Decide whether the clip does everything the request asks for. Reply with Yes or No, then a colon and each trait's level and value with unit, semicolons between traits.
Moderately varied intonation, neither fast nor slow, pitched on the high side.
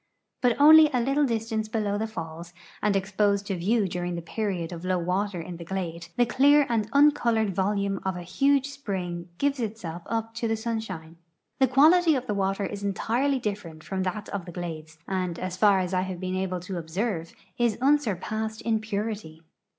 Yes: average, 4.2 semitones; average, 190 wpm; high, 200 Hz